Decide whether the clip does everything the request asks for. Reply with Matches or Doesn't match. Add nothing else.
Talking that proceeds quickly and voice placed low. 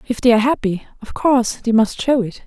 Doesn't match